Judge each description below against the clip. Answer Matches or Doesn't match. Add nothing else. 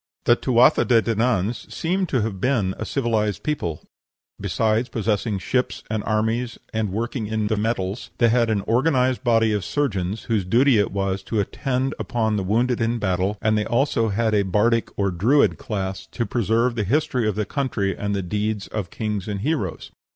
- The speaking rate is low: Doesn't match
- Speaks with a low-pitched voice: Matches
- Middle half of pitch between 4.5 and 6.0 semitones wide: Doesn't match